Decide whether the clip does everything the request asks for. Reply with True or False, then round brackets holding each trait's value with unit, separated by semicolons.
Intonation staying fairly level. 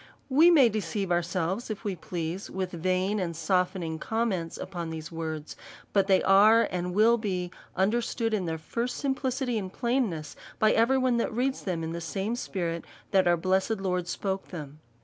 False (4.7 semitones)